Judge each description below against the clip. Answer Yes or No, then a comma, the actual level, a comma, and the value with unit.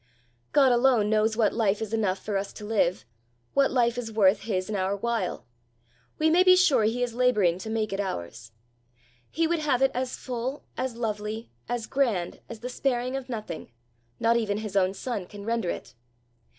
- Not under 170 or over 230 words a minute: Yes, average, 190 wpm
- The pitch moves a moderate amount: Yes, average, 3.6 semitones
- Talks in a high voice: Yes, high, 225 Hz